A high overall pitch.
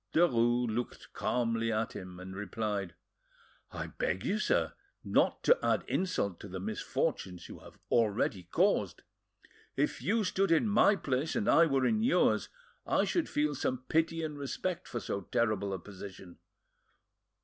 No: low, 120 Hz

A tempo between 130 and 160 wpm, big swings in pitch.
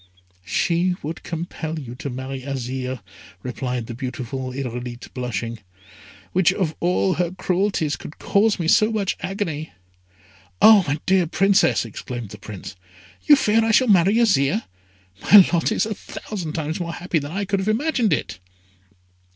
Yes: average, 155 wpm; wide, 7.2 semitones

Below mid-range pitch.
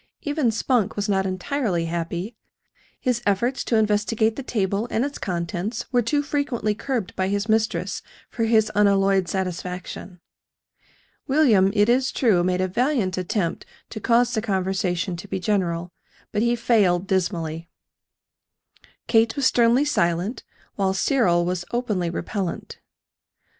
No: high, 205 Hz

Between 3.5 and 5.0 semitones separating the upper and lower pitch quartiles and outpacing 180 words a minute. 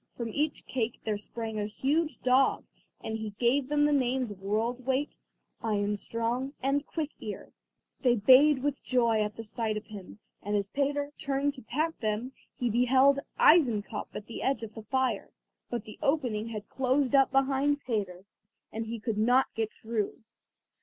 No: average, 4.0 semitones; average, 175 wpm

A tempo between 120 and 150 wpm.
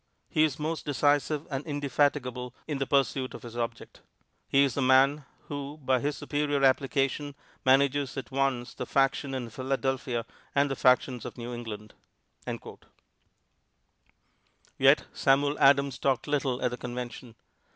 Yes: average, 140 wpm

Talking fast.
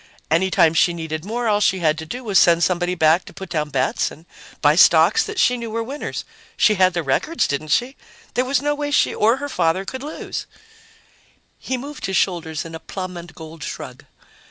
Yes: fast, 215 wpm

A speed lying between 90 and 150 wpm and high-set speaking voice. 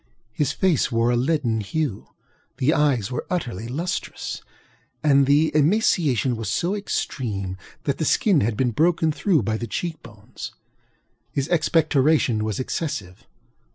No: average, 140 wpm; medium, 140 Hz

